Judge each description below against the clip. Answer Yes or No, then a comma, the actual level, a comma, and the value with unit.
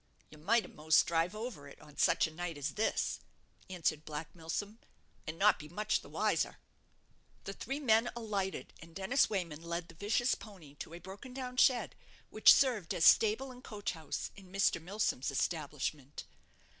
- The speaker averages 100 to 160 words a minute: No, average, 170 wpm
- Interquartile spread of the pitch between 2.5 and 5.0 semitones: No, wide, 5.5 semitones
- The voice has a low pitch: No, medium, 185 Hz